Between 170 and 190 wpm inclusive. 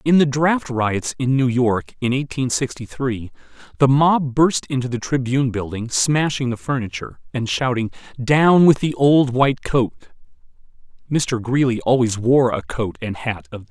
Yes: average, 175 wpm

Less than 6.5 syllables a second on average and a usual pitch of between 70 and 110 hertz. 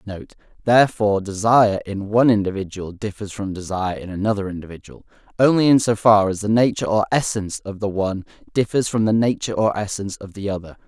No: 6.6 syllables/s; low, 105 Hz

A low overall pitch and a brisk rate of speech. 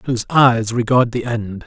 No: low, 120 Hz; average, 180 wpm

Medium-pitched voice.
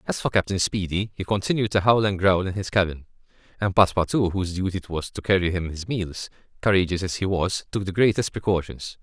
No: very low, 95 Hz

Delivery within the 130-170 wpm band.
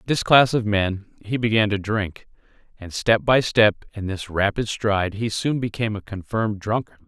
No: average, 195 wpm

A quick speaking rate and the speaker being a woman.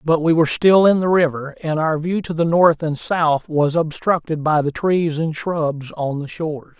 No: fast, 220 wpm; male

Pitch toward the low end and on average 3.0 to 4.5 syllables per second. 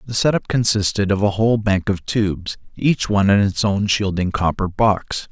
No: low, 100 Hz; 5.0 syllables/s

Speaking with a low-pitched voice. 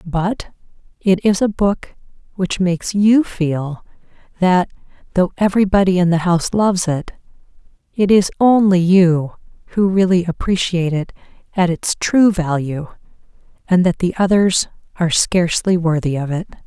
No: medium, 180 Hz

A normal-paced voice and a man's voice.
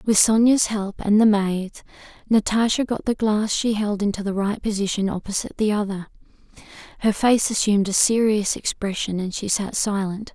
No: average, 170 wpm; female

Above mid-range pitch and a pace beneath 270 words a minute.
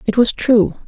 Yes: high, 225 Hz; fast, 205 wpm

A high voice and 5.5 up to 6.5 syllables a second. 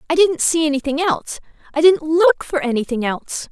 Yes: very high, 305 Hz; 5.7 syllables/s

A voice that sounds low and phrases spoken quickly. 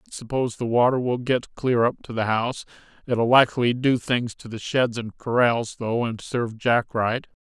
Yes: low, 120 Hz; fast, 210 wpm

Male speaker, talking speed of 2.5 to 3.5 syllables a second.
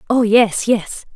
No: female; 3.4 syllables/s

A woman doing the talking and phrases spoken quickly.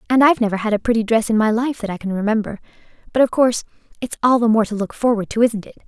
Yes: female; fast, 265 wpm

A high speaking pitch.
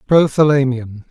No: low, 135 Hz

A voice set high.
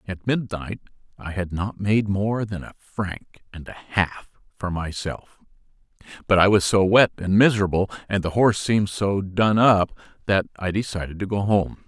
No: low, 100 Hz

